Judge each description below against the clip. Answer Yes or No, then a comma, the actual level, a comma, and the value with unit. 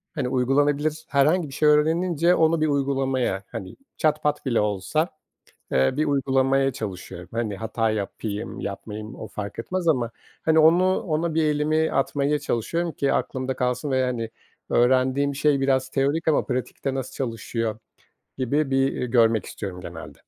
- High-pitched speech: No, low, 135 Hz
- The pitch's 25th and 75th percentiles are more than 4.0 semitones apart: Yes, average, 4.7 semitones